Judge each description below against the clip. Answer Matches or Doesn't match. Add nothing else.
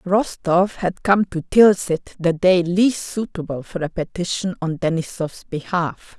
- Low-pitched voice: Doesn't match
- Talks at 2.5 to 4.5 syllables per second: Matches